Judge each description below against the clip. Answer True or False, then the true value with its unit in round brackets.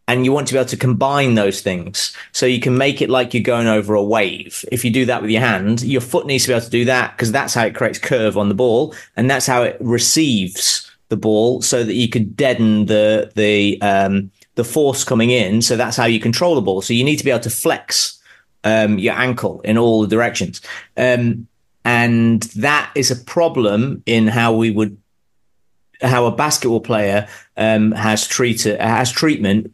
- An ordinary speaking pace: False (215 wpm)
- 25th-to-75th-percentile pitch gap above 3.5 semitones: False (2.8 semitones)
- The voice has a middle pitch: False (115 Hz)